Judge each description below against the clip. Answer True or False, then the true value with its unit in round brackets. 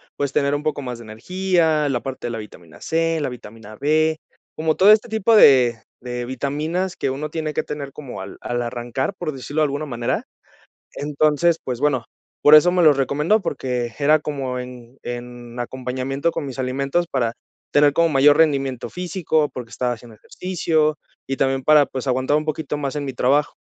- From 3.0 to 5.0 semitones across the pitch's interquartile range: True (3.7 semitones)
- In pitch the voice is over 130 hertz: True (140 Hz)